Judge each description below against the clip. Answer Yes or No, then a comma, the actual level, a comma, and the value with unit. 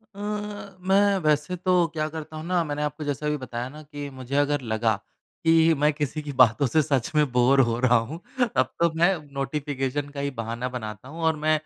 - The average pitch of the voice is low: No, medium, 145 Hz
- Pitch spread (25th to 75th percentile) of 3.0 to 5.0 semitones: Yes, average, 3.6 semitones